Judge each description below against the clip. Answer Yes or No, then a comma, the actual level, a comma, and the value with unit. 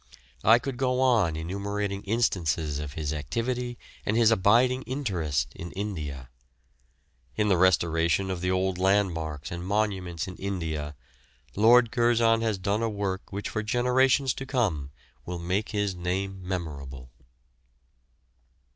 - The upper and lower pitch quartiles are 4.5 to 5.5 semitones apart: Yes, average, 5.1 semitones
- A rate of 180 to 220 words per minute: No, slow, 135 wpm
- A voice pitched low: Yes, very low, 95 Hz